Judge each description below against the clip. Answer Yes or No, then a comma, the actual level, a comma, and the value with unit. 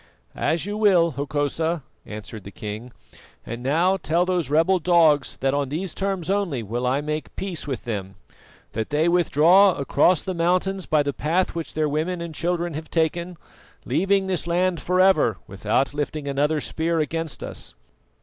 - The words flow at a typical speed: Yes, average, 170 wpm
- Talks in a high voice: No, medium, 160 Hz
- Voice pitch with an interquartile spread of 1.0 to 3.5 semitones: No, average, 4.1 semitones